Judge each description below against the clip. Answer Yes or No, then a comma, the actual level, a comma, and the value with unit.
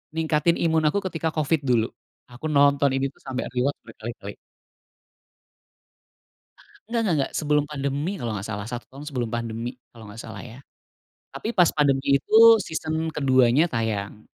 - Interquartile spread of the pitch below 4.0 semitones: No, average, 4.4 semitones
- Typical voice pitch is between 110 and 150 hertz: Yes, low, 135 Hz